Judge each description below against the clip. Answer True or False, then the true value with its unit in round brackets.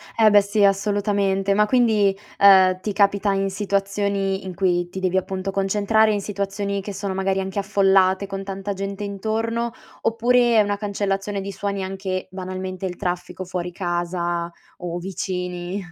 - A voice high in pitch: True (195 Hz)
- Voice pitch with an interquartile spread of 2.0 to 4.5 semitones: False (1.3 semitones)